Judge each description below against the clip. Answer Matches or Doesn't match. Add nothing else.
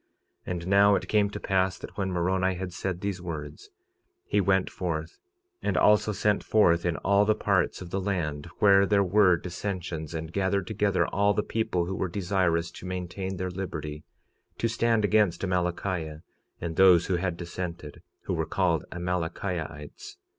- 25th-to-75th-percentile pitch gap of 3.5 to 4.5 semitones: Doesn't match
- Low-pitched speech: Matches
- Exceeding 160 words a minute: Matches